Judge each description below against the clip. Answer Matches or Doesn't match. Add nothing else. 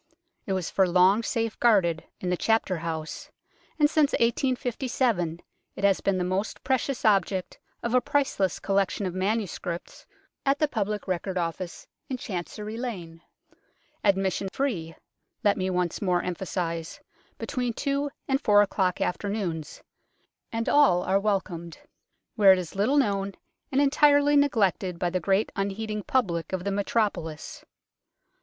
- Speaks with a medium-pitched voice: Doesn't match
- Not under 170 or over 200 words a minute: Doesn't match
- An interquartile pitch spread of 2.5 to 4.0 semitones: Doesn't match